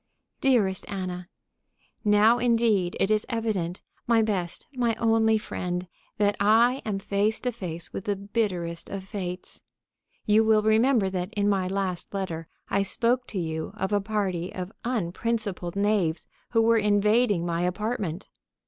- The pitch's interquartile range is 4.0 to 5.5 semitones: No, average, 3.4 semitones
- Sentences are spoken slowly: No, average, 150 wpm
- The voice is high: Yes, high, 205 Hz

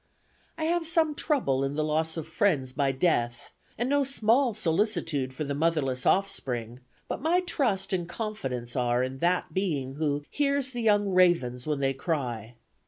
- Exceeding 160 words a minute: Yes, average, 170 wpm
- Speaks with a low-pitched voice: No, medium, 160 Hz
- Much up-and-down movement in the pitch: Yes, wide, 8.4 semitones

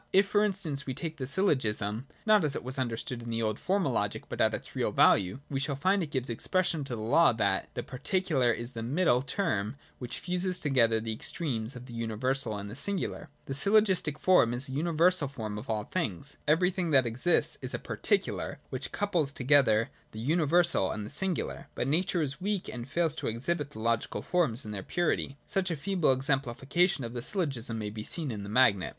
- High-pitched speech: No, low, 135 Hz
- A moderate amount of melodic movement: No, wide, 6.8 semitones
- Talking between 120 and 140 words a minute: No, fast, 205 wpm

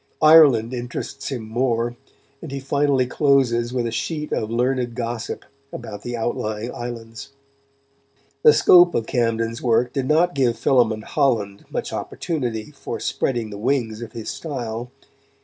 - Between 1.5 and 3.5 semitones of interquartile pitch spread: Yes, average, 3.1 semitones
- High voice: No, low, 120 Hz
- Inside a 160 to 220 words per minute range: No, average, 145 wpm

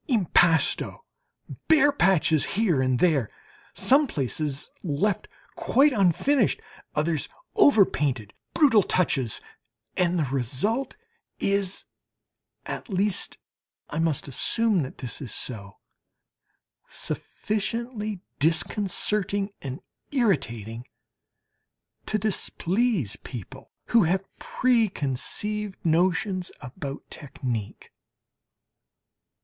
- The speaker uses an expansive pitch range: Yes, wide, 7.4 semitones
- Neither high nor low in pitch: Yes, medium, 180 Hz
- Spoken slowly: Yes, slow, 85 wpm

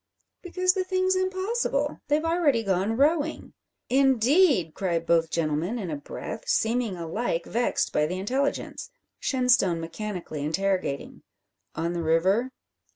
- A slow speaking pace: Yes, slow, 125 wpm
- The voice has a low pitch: No, high, 225 Hz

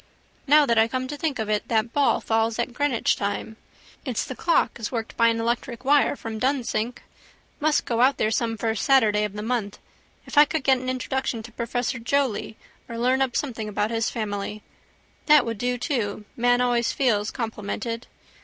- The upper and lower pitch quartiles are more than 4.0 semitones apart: No, average, 2.8 semitones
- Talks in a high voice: Yes, high, 235 Hz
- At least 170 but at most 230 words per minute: Yes, average, 190 wpm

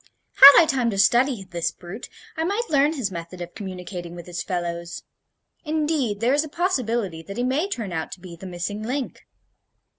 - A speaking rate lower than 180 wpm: No, average, 190 wpm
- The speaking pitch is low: No, high, 210 Hz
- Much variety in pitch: Yes, wide, 7.9 semitones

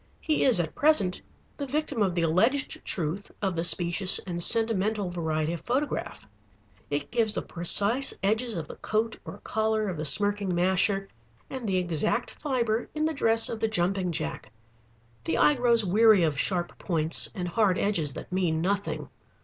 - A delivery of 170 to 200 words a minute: Yes, average, 175 wpm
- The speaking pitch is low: No, high, 195 Hz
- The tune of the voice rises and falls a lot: No, average, 4.7 semitones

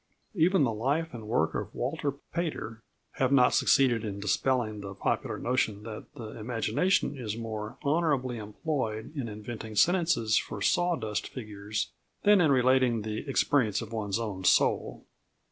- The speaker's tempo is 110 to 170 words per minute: Yes, average, 145 wpm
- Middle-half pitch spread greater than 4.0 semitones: Yes, average, 4.7 semitones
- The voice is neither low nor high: No, low, 115 Hz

